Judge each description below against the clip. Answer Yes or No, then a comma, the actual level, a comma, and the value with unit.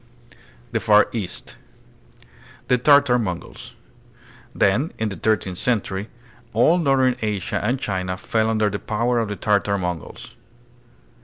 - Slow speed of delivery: Yes, slow, 130 wpm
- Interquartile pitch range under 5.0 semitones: Yes, average, 3.9 semitones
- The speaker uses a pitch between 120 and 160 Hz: No, low, 110 Hz